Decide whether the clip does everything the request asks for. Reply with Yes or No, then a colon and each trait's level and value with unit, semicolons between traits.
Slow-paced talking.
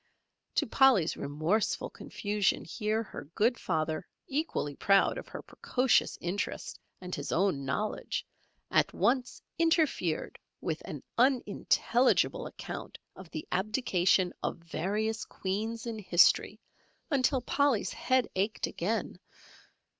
Yes: slow, 115 wpm